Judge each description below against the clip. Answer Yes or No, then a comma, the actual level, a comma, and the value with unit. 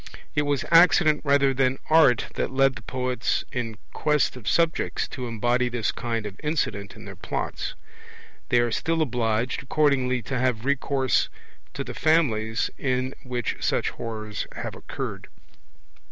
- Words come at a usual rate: Yes, average, 150 wpm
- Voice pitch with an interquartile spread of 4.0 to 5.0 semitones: No, average, 3.6 semitones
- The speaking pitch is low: Yes, low, 125 Hz